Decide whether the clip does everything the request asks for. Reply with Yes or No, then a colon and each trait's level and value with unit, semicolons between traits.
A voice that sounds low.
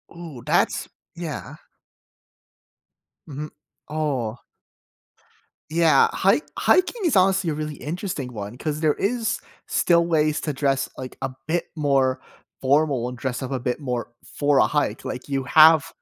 No: medium, 150 Hz